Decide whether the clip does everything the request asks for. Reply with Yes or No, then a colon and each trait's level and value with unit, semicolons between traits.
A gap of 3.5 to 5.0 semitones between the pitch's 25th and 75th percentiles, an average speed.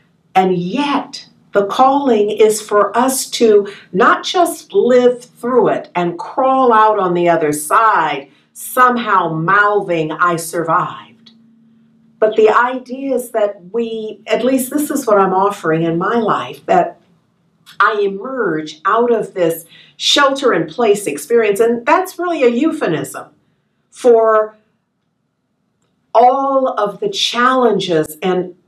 No: average, 4.7 semitones; slow, 130 wpm